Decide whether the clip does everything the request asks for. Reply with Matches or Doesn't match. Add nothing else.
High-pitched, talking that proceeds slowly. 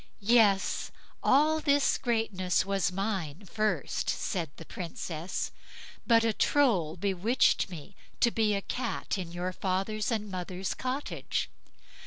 Matches